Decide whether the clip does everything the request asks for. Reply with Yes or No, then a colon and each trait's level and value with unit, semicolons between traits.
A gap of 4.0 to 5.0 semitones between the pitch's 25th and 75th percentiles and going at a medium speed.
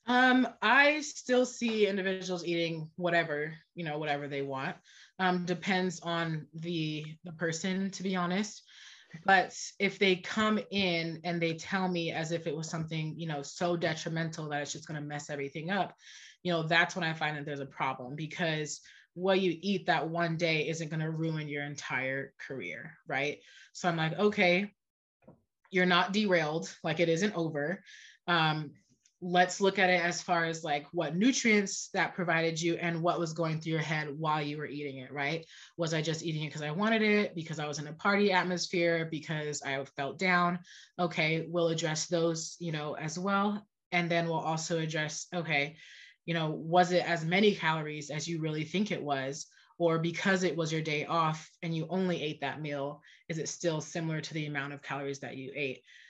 No: average, 2.8 semitones; average, 195 wpm